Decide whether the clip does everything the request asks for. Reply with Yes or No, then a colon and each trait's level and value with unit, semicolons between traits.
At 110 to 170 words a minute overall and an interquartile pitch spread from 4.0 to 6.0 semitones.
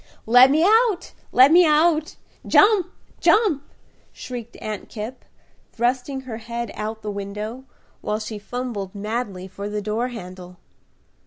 Yes: average, 140 wpm; average, 4.5 semitones